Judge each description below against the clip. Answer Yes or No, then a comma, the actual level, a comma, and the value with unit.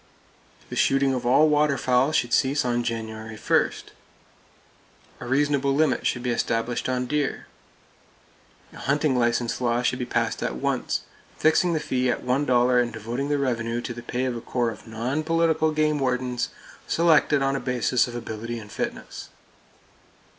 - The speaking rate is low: No, average, 165 wpm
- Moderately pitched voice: No, low, 125 Hz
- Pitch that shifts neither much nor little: Yes, average, 3.2 semitones